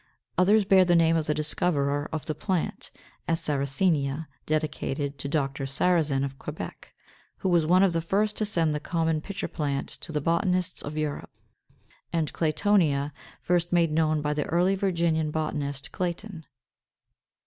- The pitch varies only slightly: No, average, 3.2 semitones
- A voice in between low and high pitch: Yes, medium, 160 Hz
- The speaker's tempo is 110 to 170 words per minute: Yes, average, 160 wpm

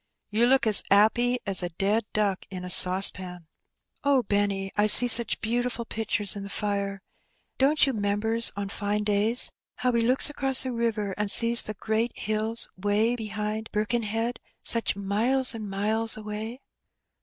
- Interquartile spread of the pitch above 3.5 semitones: No, narrow, 2.6 semitones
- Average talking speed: Yes, average, 165 wpm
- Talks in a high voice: Yes, high, 215 Hz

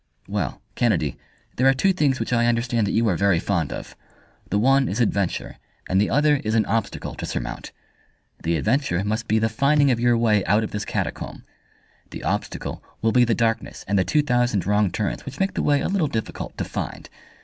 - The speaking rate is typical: No, fast, 210 wpm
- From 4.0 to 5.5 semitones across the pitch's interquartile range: Yes, average, 4.3 semitones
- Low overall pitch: Yes, low, 115 Hz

